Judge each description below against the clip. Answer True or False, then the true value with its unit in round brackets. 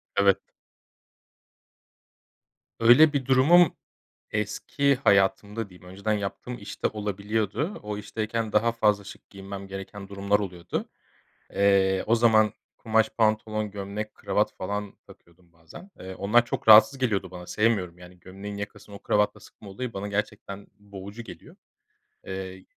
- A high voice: False (105 Hz)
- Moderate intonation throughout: False (2.3 semitones)